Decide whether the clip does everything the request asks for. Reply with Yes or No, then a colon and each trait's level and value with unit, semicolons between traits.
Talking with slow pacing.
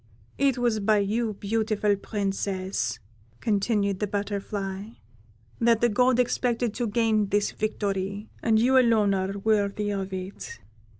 Yes: slow, 130 wpm